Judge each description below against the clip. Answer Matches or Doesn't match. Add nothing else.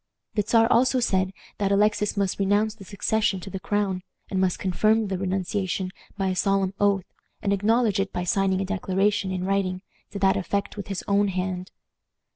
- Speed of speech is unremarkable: Matches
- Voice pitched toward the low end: Doesn't match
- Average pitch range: Doesn't match